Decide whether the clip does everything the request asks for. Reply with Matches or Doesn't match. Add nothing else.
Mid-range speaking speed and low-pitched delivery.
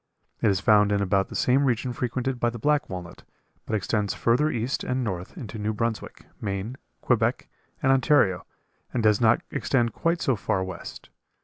Matches